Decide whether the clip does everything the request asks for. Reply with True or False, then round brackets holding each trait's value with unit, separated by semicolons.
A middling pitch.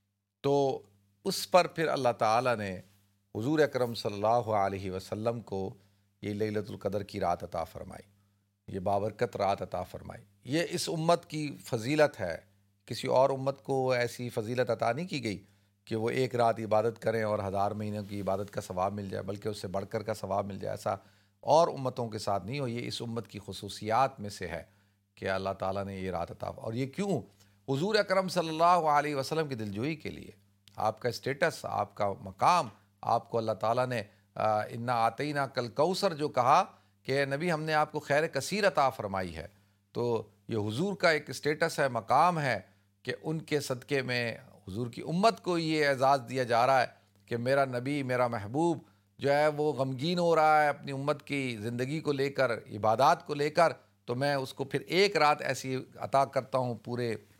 False (120 Hz)